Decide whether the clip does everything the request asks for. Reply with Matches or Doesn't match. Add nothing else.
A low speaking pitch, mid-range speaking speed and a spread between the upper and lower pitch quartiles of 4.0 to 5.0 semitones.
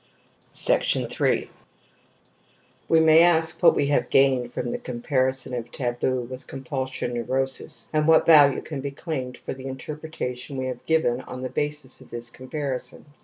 Doesn't match